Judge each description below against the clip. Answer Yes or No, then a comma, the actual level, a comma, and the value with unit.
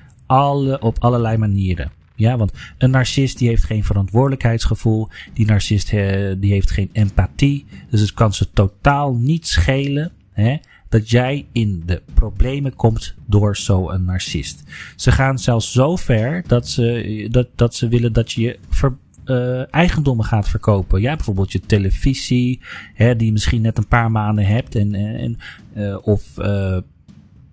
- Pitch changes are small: No, average, 3.8 semitones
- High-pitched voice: No, low, 110 Hz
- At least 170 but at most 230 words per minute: No, average, 155 wpm